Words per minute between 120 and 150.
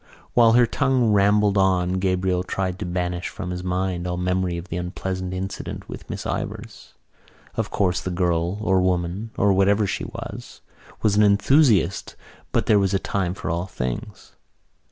No: average, 170 wpm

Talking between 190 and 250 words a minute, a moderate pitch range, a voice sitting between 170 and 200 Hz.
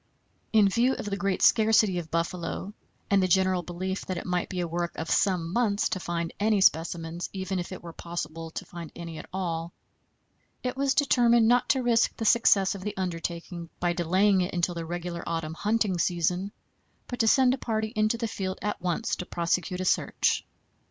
Yes: average, 200 wpm; average, 3.6 semitones; medium, 185 Hz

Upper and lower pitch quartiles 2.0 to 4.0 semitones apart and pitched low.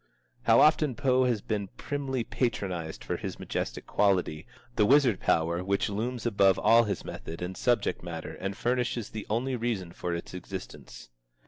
No: average, 5.1 semitones; low, 105 Hz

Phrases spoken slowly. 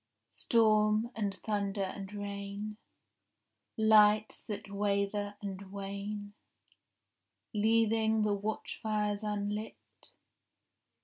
Yes: slow, 80 wpm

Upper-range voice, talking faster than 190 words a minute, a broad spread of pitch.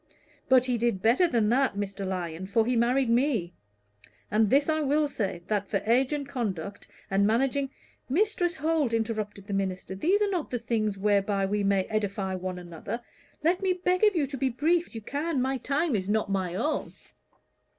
Yes: high, 230 Hz; average, 200 wpm; wide, 6.1 semitones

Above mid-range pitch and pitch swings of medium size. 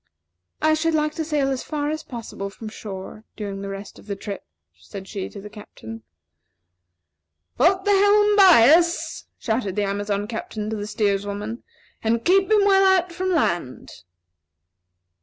No: high, 230 Hz; wide, 8.8 semitones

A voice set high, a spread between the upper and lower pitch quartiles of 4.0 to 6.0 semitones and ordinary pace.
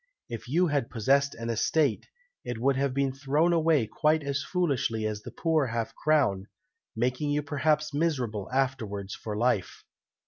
No: low, 135 Hz; average, 4.7 semitones; average, 160 wpm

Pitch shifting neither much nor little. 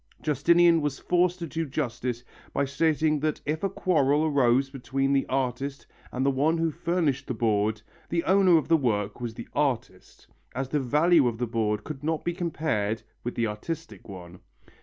Yes: average, 5.0 semitones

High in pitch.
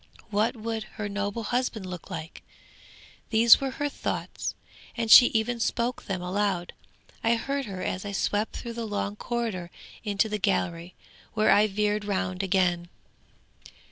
Yes: high, 210 Hz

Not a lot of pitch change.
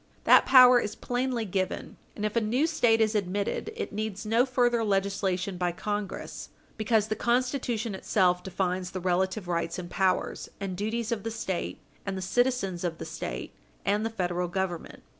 No: average, 3.7 semitones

